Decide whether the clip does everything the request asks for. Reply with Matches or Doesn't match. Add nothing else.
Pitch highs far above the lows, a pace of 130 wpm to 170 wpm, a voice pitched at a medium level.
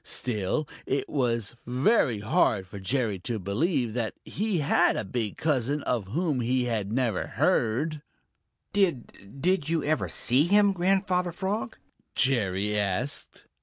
Doesn't match